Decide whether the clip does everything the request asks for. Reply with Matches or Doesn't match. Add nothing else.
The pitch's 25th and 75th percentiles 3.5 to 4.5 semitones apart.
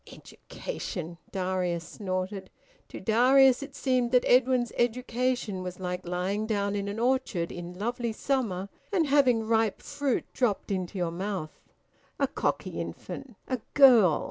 Doesn't match